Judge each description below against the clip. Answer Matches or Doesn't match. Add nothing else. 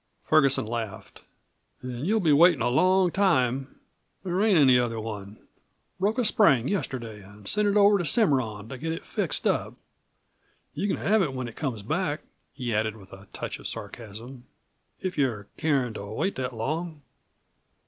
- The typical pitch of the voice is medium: Doesn't match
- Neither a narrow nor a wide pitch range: Doesn't match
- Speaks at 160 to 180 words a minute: Matches